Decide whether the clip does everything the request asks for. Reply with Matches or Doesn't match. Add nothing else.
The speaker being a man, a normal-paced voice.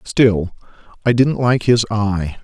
Matches